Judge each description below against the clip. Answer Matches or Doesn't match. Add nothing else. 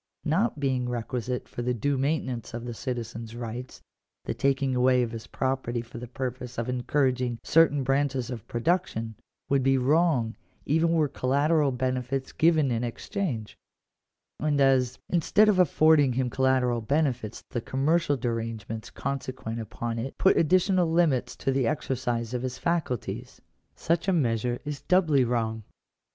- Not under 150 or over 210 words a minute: Matches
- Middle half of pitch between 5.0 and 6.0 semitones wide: Doesn't match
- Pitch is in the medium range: Doesn't match